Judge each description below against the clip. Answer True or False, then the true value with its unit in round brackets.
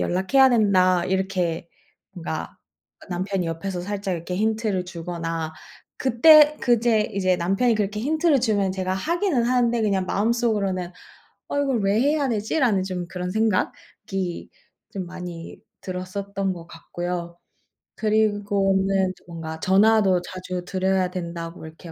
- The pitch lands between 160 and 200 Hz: True (190 Hz)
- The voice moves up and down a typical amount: True (3.5 semitones)